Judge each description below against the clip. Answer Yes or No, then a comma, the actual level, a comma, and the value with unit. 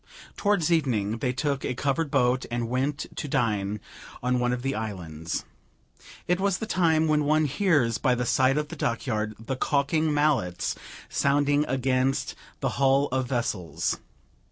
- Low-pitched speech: Yes, low, 130 Hz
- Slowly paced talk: No, average, 155 wpm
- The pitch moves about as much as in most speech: Yes, average, 4.0 semitones